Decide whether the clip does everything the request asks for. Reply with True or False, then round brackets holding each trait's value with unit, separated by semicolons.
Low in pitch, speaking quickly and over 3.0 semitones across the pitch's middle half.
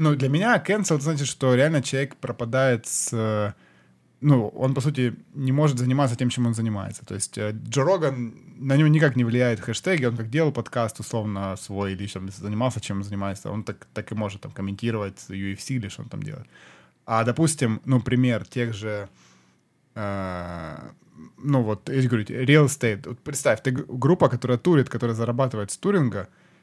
True (120 Hz; 180 wpm; 4.6 semitones)